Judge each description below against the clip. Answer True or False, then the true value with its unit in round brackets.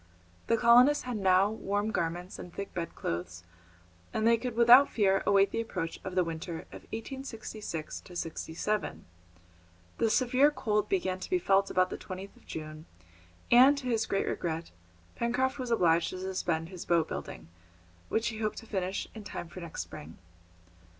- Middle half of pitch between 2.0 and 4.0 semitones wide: False (5.1 semitones)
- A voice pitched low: False (195 Hz)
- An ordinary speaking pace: True (165 wpm)